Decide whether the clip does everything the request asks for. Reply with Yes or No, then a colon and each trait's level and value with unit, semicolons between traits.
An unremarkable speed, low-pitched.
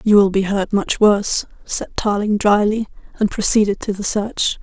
No: average, 180 wpm; high, 205 Hz